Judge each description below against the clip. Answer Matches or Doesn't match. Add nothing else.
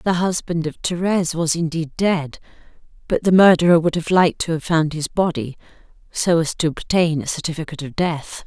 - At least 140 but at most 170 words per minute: Doesn't match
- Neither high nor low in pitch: Matches